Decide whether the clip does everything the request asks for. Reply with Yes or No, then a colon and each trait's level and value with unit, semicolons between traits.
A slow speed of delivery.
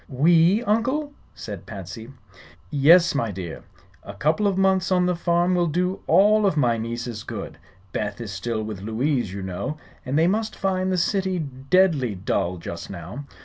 No: average, 170 wpm